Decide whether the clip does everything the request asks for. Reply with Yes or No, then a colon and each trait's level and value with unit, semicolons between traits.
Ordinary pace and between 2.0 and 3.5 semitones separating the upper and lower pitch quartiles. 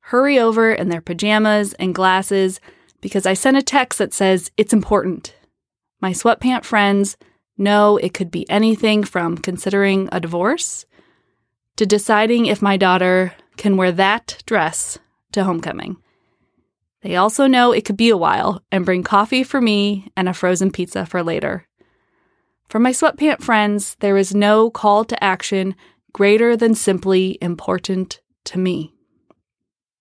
Yes: average, 150 wpm; average, 2.9 semitones